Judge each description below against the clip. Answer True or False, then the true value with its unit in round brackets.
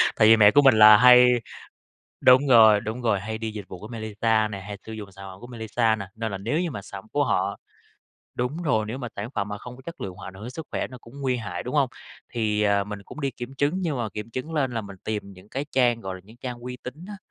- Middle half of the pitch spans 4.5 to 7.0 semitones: False (3.5 semitones)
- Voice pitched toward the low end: True (110 Hz)